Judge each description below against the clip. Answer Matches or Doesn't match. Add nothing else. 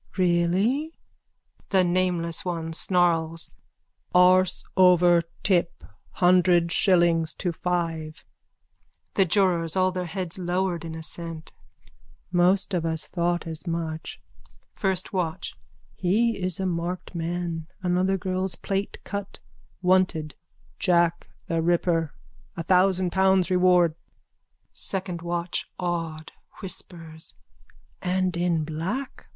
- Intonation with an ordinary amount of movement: Doesn't match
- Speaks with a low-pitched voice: Doesn't match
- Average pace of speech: Doesn't match